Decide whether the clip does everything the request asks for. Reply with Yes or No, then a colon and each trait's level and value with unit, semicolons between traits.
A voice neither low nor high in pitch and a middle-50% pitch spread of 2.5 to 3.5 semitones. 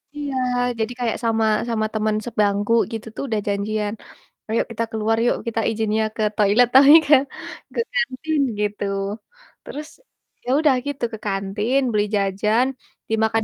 No: high, 220 Hz; average, 2.8 semitones